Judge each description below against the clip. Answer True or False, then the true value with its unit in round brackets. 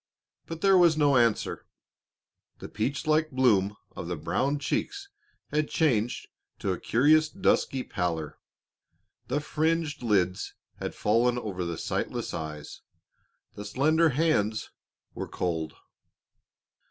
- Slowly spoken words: True (120 wpm)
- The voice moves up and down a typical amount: False (8.3 semitones)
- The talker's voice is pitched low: True (125 Hz)